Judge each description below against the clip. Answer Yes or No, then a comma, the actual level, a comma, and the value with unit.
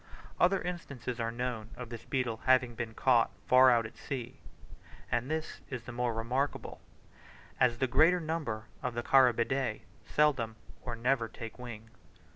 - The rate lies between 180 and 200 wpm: No, average, 155 wpm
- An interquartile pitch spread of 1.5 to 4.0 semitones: Yes, narrow, 2.6 semitones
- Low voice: Yes, low, 125 Hz